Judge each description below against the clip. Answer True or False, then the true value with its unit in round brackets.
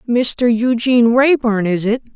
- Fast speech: False (140 wpm)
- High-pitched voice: True (235 Hz)